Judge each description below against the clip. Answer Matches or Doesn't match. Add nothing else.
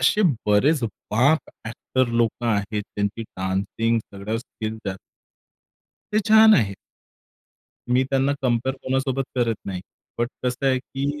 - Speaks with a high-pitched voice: Doesn't match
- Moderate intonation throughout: Matches